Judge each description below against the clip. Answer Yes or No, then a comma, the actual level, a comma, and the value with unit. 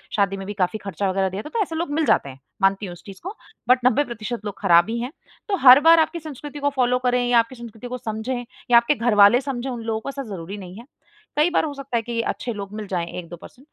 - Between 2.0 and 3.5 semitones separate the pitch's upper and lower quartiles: No, average, 5.1 semitones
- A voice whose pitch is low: No, high, 235 Hz